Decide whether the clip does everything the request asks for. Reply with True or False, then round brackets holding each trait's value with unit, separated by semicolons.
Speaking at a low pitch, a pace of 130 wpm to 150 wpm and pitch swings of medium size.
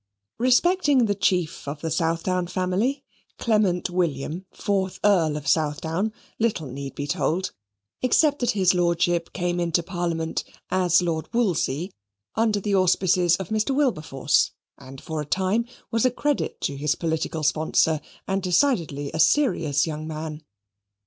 False (175 Hz; 140 wpm; 4.4 semitones)